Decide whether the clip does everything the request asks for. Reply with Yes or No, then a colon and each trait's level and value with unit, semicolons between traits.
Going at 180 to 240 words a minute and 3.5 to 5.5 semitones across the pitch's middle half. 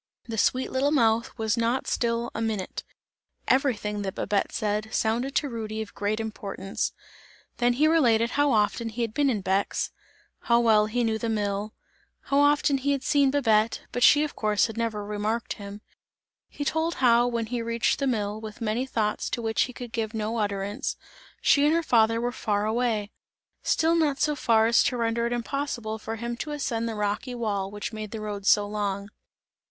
No: average, 195 wpm; average, 2.9 semitones